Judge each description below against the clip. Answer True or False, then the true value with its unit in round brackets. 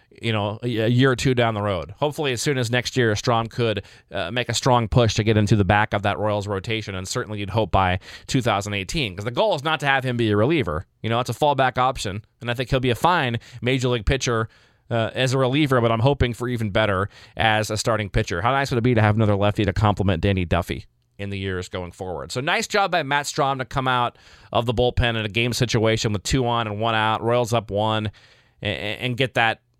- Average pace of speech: False (250 wpm)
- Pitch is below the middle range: True (115 Hz)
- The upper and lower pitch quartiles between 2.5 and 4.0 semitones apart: True (3.1 semitones)